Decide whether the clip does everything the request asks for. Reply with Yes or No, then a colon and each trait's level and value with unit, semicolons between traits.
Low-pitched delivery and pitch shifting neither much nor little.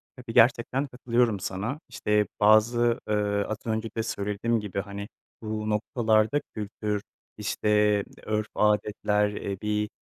No: low, 105 Hz; narrow, 1.5 semitones